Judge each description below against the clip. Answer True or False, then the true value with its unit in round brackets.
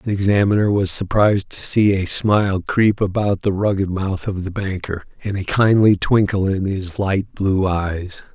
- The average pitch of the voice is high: False (100 Hz)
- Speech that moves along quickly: False (180 wpm)